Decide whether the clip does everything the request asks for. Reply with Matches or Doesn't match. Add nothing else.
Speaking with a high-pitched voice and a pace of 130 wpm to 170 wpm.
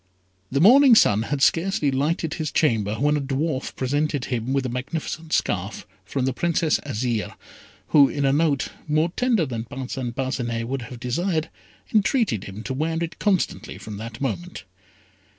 Doesn't match